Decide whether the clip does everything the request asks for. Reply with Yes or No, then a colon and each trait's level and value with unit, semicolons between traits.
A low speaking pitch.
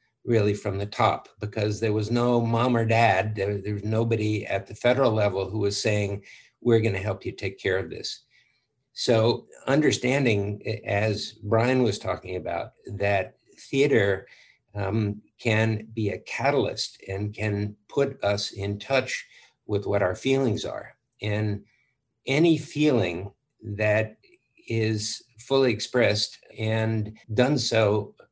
Yes: low, 110 Hz